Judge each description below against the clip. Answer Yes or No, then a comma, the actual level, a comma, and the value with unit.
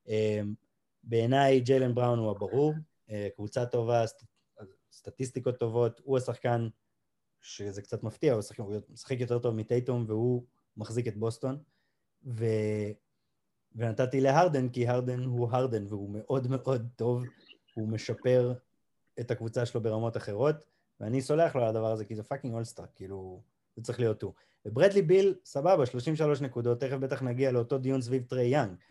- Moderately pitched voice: No, low, 120 Hz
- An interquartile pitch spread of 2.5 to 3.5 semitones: Yes, average, 3.0 semitones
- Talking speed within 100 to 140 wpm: No, fast, 150 wpm